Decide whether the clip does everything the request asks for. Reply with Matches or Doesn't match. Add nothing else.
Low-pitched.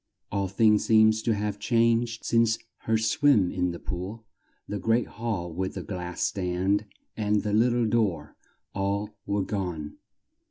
Matches